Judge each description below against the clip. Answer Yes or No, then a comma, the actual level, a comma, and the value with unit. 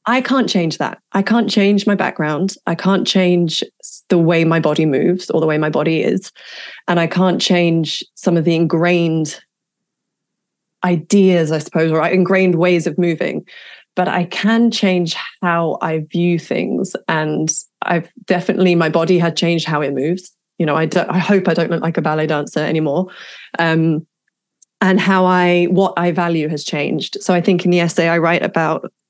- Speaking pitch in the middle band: Yes, medium, 175 Hz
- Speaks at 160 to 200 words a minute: Yes, average, 185 wpm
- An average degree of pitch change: No, narrow, 2.3 semitones